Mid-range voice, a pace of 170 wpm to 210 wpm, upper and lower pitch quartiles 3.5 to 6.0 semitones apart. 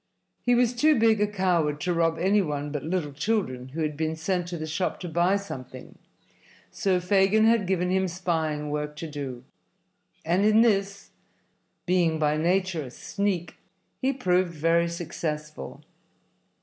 No: medium, 175 Hz; average, 160 wpm; average, 4.1 semitones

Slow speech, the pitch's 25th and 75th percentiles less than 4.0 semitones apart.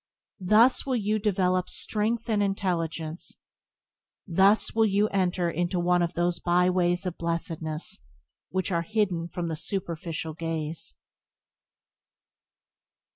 Yes: slow, 110 wpm; average, 3.0 semitones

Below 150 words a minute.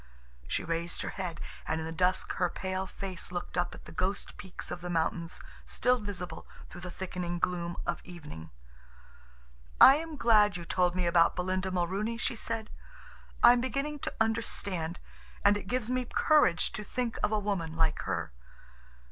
No: average, 175 wpm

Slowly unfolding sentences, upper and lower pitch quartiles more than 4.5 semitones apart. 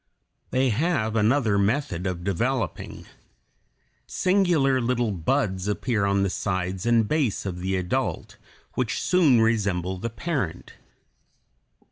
Yes: slow, 115 wpm; wide, 5.5 semitones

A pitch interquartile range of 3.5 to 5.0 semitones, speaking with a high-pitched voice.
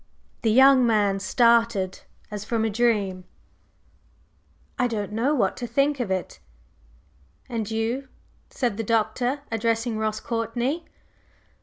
No: narrow, 2.5 semitones; high, 230 Hz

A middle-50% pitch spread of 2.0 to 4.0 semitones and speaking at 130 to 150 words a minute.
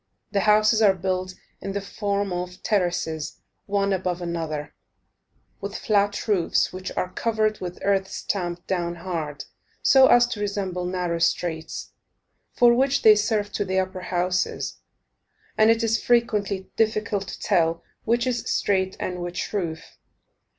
Yes: average, 3.0 semitones; average, 145 wpm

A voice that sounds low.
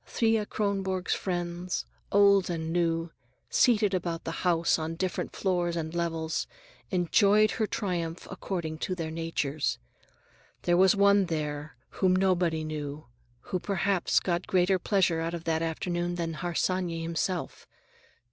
No: medium, 175 Hz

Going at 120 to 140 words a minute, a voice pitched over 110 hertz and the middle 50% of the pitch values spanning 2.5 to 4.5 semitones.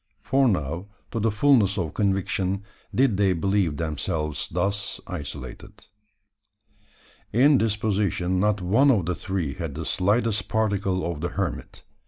No: slow, 135 wpm; very low, 95 Hz; average, 3.4 semitones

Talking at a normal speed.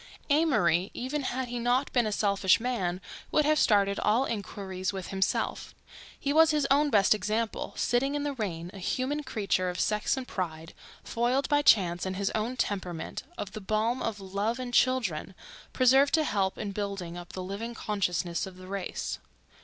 Yes: average, 175 wpm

